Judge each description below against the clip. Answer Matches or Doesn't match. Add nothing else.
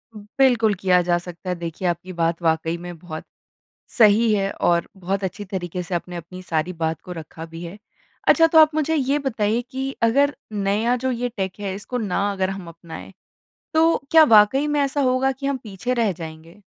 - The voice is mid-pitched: Doesn't match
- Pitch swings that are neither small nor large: Doesn't match